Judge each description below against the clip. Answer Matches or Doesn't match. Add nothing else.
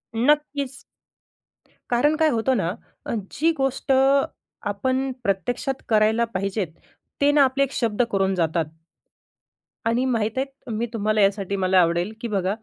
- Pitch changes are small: Doesn't match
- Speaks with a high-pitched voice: Matches